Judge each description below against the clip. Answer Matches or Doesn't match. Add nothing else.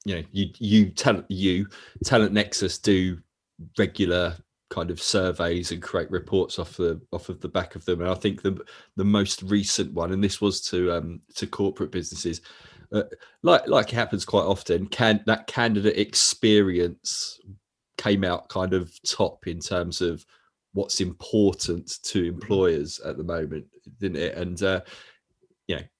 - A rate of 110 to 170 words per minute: Matches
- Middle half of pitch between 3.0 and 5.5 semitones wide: Doesn't match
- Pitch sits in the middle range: Doesn't match